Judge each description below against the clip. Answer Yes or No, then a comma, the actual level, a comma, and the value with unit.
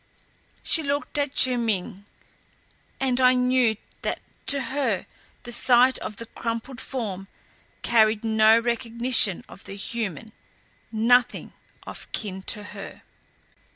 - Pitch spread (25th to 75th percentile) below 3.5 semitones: Yes, average, 2.7 semitones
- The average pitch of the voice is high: Yes, high, 230 Hz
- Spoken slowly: Yes, slow, 120 wpm